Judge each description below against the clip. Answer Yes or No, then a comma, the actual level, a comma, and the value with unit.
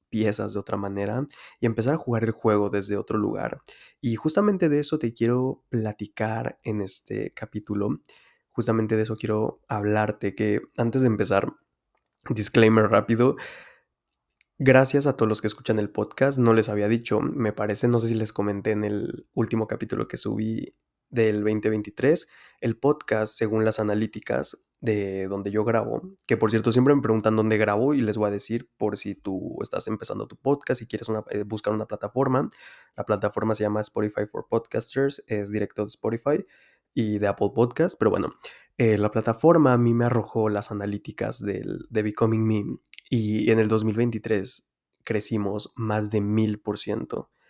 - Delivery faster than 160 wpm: Yes, average, 170 wpm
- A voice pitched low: Yes, low, 110 Hz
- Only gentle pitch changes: Yes, narrow, 1.8 semitones